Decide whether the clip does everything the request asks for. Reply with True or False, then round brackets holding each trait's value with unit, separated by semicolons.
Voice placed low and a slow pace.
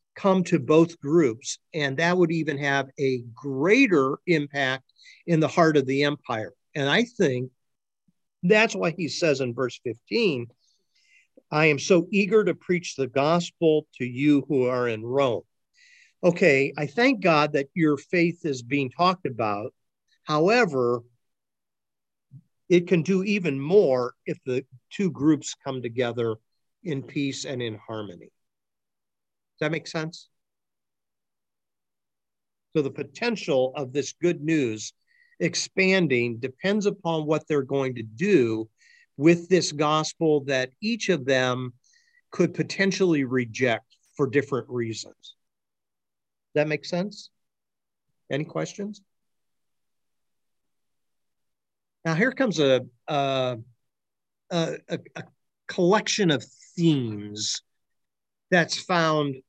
False (150 Hz; 120 wpm)